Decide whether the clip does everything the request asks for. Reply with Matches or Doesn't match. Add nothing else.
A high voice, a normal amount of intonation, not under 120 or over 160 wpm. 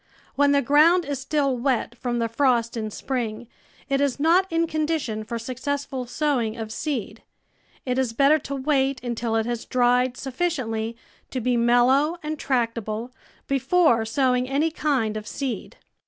Matches